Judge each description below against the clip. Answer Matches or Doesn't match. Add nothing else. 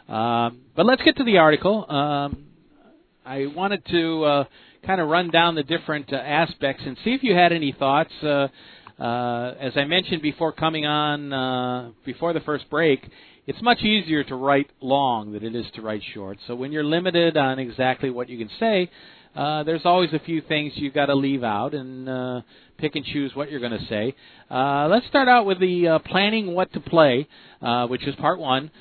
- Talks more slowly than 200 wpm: Doesn't match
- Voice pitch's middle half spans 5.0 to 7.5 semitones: Doesn't match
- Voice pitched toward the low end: Doesn't match